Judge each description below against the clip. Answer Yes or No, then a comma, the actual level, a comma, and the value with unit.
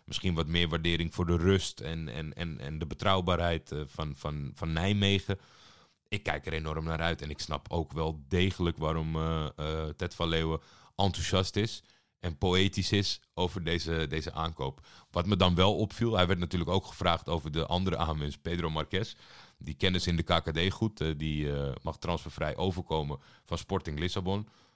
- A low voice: Yes, very low, 85 Hz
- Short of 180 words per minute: No, average, 185 wpm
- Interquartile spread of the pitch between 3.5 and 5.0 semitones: No, average, 3.1 semitones